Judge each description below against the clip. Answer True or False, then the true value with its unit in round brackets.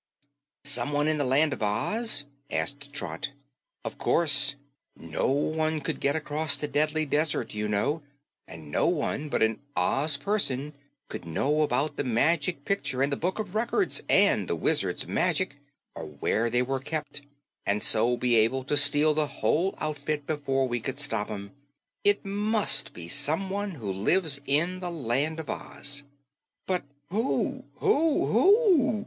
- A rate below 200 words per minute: True (155 wpm)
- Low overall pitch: False (145 Hz)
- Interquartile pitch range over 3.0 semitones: True (4.0 semitones)